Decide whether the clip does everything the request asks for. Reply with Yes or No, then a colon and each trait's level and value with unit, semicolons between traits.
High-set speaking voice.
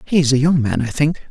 No: medium, 145 Hz